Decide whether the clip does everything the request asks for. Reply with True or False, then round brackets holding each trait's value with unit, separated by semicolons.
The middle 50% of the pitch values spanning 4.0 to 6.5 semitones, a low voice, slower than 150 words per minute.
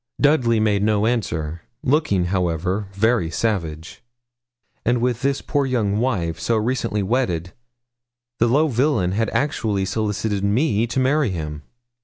True (4.8 semitones; 110 Hz; 135 wpm)